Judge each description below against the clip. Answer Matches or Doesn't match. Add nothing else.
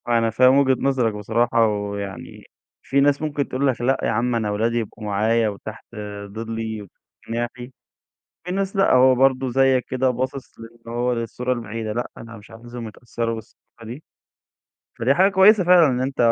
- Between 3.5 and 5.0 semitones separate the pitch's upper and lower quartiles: Doesn't match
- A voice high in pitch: Doesn't match